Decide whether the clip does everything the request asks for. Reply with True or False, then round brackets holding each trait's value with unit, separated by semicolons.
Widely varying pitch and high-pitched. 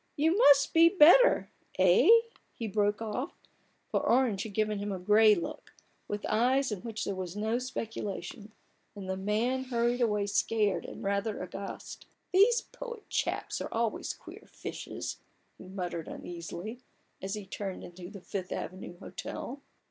False (3.9 semitones; 210 Hz)